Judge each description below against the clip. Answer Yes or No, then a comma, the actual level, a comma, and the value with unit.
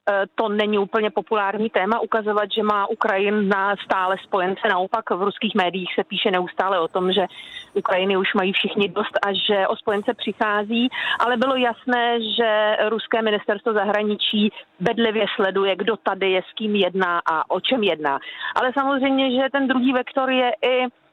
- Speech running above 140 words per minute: Yes, average, 165 wpm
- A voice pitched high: Yes, high, 215 Hz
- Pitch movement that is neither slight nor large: Yes, average, 3.0 semitones